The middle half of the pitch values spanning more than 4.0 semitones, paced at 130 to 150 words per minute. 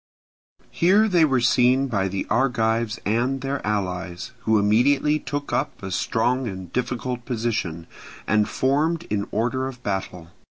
Yes: average, 4.5 semitones; average, 145 wpm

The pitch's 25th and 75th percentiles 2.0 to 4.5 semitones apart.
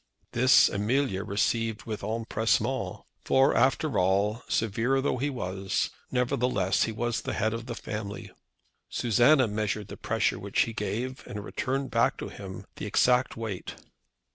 Yes: average, 3.4 semitones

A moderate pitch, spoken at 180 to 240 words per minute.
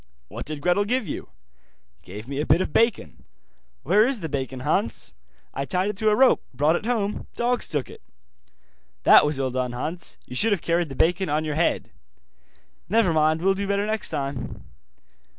Yes: medium, 170 Hz; average, 190 wpm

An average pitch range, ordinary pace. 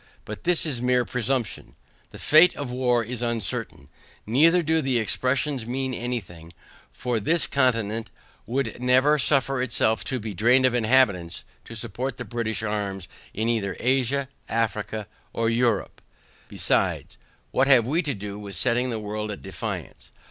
Yes: average, 3.3 semitones; average, 155 wpm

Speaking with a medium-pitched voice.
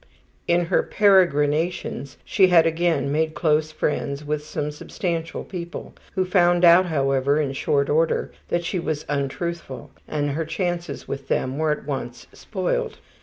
Yes: medium, 160 Hz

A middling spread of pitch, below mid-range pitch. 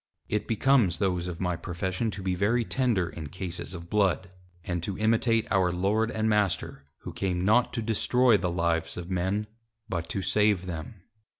Yes: average, 3.6 semitones; very low, 95 Hz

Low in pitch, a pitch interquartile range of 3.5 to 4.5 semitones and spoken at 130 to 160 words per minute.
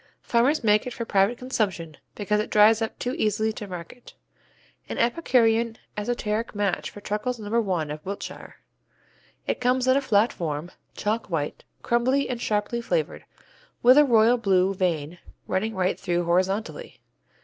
No: high, 215 Hz; average, 3.9 semitones; average, 155 wpm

